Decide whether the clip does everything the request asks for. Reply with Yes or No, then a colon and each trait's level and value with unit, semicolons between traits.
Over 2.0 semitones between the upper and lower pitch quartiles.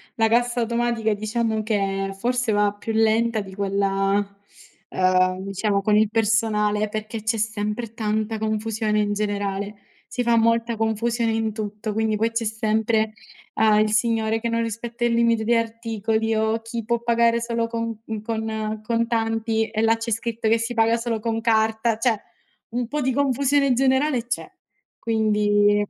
No: narrow, 1.5 semitones